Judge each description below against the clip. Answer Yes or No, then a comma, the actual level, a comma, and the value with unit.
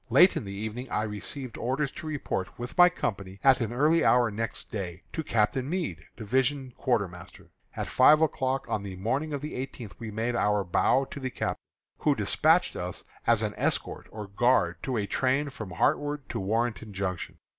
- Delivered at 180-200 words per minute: Yes, average, 190 wpm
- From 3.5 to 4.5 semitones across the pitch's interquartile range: No, average, 4.9 semitones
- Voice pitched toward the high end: No, low, 120 Hz